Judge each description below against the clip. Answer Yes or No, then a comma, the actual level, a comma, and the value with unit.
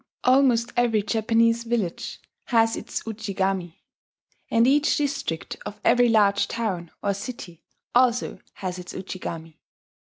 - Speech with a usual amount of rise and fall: Yes, average, 3.9 semitones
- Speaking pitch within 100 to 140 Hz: No, high, 225 Hz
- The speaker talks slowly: Yes, slow, 120 wpm